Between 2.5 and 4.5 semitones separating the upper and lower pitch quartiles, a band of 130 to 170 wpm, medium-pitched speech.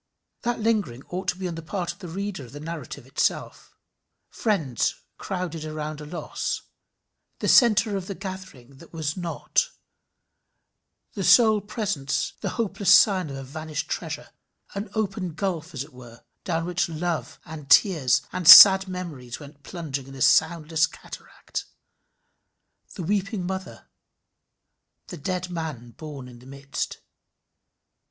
No: average, 5.0 semitones; average, 145 wpm; medium, 165 Hz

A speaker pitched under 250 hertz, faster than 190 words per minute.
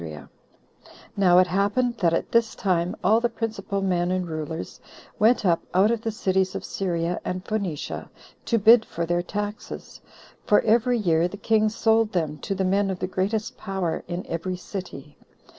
No: high, 190 Hz; average, 175 wpm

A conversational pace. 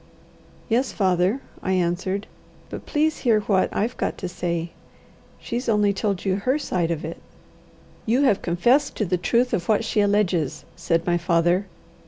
Yes: average, 165 wpm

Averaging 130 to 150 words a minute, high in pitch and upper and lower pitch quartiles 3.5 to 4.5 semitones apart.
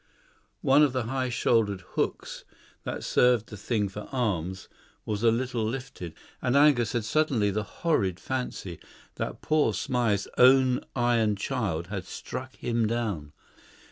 No: average, 140 wpm; low, 115 Hz; average, 3.9 semitones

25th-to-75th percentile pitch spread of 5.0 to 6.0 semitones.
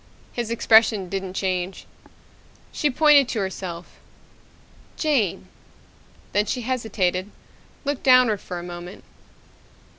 Yes: wide, 5.4 semitones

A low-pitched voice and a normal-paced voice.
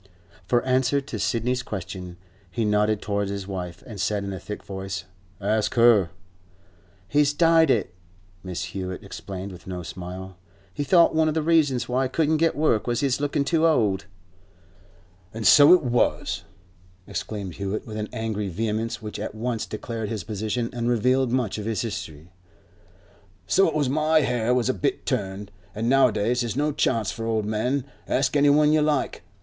Yes: low, 115 Hz; average, 175 wpm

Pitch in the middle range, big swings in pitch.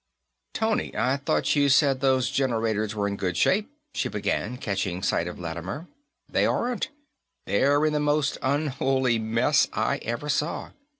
No: low, 130 Hz; wide, 5.7 semitones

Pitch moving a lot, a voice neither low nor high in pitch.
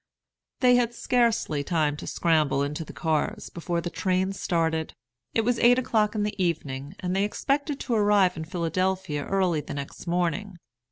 No: average, 4.6 semitones; medium, 180 Hz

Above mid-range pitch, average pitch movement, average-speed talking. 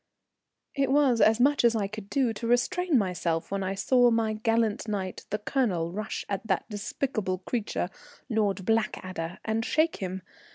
Yes: high, 220 Hz; average, 3.8 semitones; average, 170 wpm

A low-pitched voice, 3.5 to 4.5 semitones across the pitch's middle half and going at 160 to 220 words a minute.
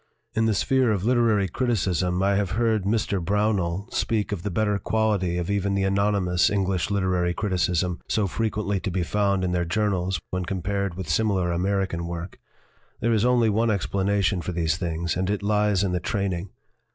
No: low, 100 Hz; average, 2.7 semitones; average, 190 wpm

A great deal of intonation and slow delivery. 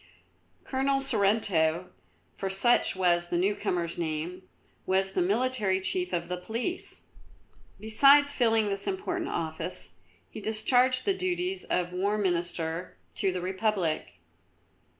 Yes: wide, 6.3 semitones; slow, 120 wpm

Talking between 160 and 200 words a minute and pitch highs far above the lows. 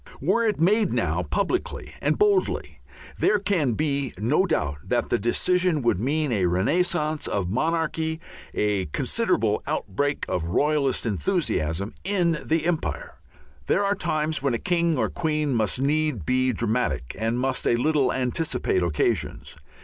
No: average, 145 wpm; wide, 6.3 semitones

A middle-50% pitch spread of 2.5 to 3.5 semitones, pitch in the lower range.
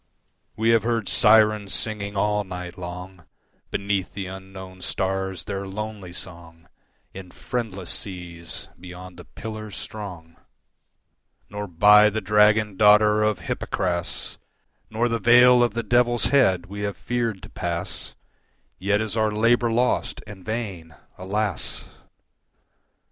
Yes: average, 2.8 semitones; low, 100 Hz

